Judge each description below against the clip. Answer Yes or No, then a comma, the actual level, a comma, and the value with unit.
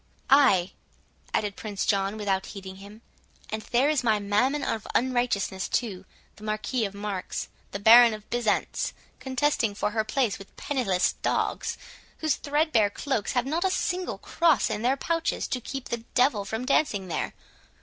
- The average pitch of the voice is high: Yes, high, 225 Hz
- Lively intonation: No, average, 4.7 semitones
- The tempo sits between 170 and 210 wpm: No, average, 155 wpm